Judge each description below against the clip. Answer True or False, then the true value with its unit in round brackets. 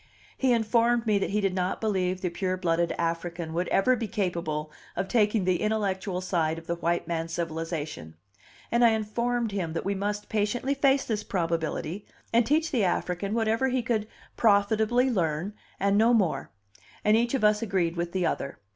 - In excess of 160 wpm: True (180 wpm)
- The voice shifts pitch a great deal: False (4.6 semitones)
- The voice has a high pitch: True (200 Hz)